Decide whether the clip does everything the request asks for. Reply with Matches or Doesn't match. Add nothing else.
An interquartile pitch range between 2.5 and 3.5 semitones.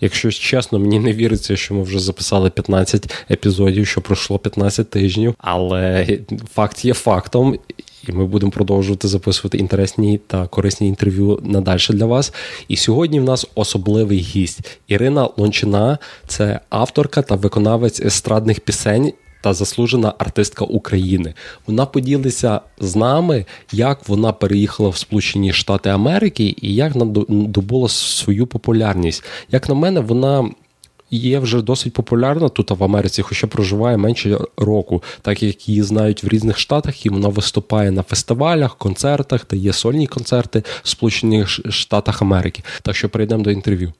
Matches